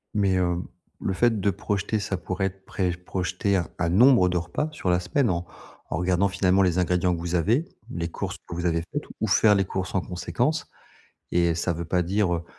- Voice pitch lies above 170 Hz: No, very low, 90 Hz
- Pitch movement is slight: Yes, narrow, 2.2 semitones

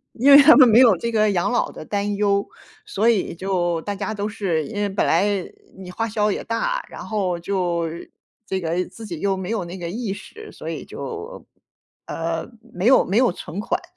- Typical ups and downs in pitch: Yes, average, 4.0 semitones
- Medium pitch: No, high, 200 Hz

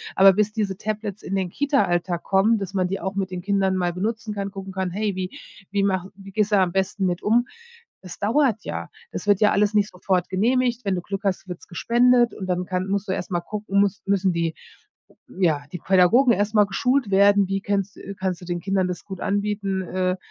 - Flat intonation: Yes, narrow, 2.1 semitones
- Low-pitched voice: No, high, 195 Hz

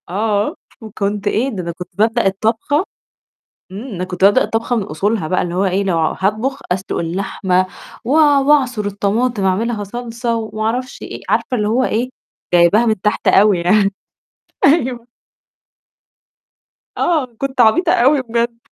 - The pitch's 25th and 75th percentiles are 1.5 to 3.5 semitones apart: No, average, 3.9 semitones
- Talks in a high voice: Yes, high, 215 Hz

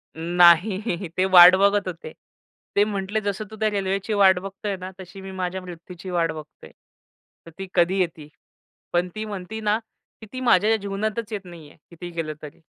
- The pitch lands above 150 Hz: Yes, high, 190 Hz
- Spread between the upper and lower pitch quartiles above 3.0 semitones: No, average, 2.7 semitones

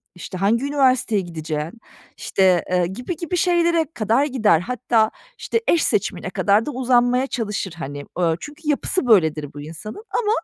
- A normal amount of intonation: No, wide, 7.3 semitones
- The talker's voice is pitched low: No, high, 220 Hz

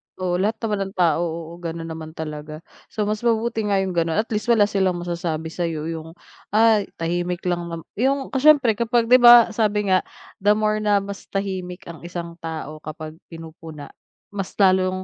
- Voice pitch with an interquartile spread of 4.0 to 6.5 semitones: Yes, average, 4.4 semitones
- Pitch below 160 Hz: No, medium, 185 Hz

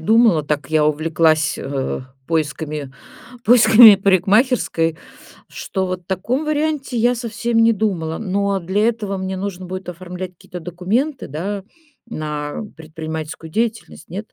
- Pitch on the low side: No, medium, 185 Hz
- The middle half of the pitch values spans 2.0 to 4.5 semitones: No, wide, 5.6 semitones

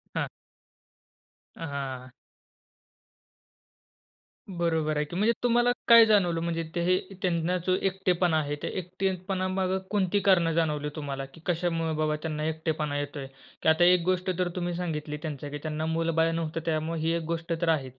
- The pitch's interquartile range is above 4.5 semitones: No, average, 2.8 semitones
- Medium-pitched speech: Yes, medium, 165 Hz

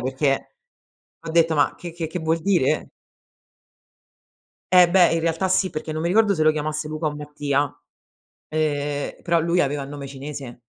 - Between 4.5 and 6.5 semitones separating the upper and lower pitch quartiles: No, narrow, 2.6 semitones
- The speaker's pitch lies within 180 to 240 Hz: No, medium, 155 Hz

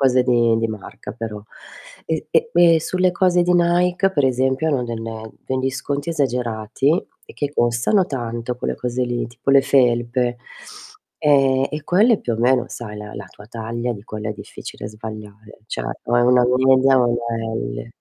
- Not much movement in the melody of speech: No, average, 3.8 semitones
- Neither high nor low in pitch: No, low, 125 Hz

